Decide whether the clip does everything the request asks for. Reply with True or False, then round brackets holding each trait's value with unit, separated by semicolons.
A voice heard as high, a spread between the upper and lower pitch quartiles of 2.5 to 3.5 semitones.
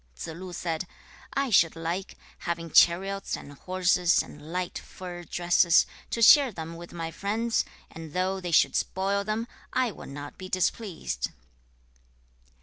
False (180 Hz; 2.9 semitones)